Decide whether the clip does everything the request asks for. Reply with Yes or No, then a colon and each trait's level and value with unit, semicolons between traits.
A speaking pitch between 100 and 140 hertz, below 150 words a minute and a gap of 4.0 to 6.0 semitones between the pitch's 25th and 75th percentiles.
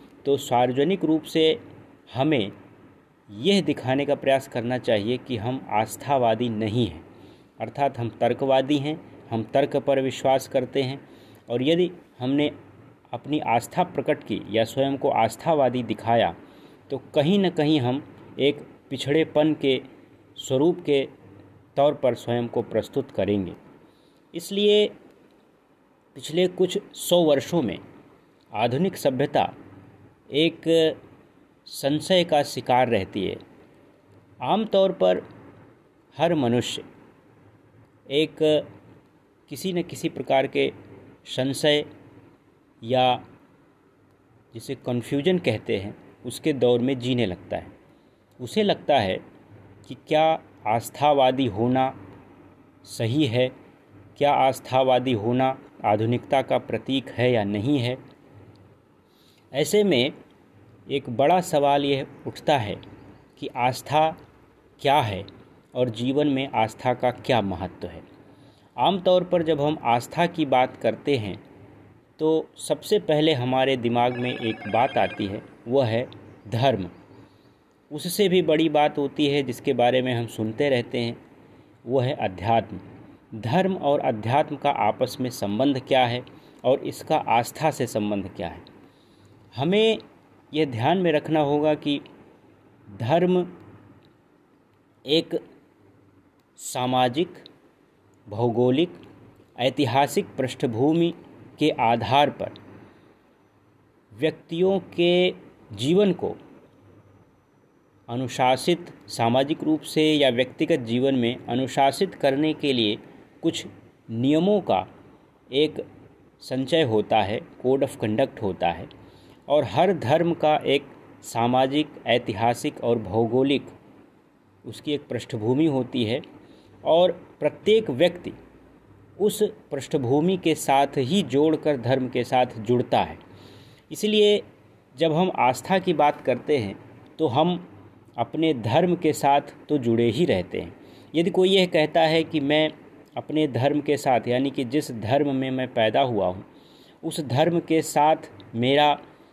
Yes: low, 135 Hz; average, 120 wpm; average, 4.4 semitones